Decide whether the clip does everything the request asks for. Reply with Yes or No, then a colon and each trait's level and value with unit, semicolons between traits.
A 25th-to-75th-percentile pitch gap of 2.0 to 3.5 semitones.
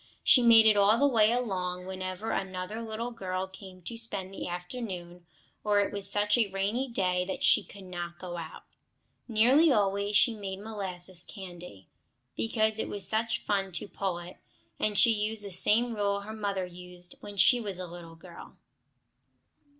Yes: average, 3.1 semitones